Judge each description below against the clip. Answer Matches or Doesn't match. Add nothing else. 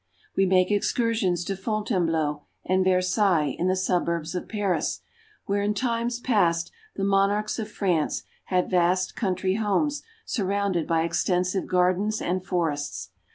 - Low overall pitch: Doesn't match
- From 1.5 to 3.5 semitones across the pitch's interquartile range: Matches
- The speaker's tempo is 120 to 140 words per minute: Matches